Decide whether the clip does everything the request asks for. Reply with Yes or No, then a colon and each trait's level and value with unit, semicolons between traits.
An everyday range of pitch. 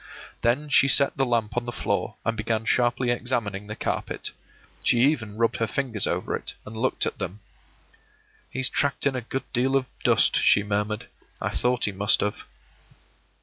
Yes: average, 3.4 semitones